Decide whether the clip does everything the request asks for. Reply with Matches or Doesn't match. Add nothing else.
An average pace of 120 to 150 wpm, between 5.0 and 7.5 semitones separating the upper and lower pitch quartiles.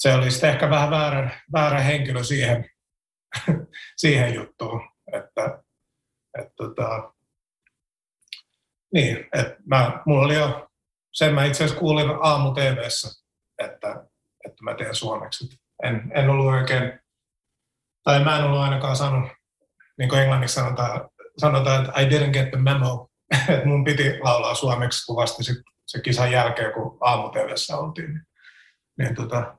Doesn't match